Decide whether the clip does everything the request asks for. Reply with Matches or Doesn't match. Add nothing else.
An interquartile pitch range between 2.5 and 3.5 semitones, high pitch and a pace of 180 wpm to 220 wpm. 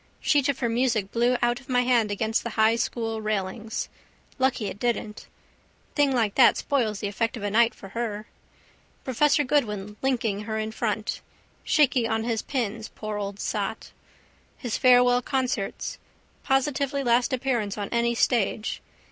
Doesn't match